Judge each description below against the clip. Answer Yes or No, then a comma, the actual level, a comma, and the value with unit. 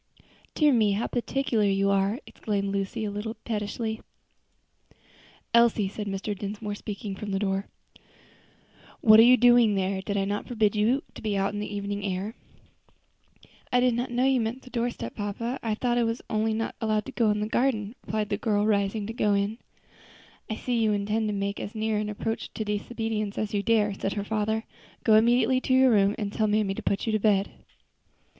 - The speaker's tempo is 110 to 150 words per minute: No, fast, 205 wpm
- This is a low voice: No, high, 215 Hz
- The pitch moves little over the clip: Yes, narrow, 2.1 semitones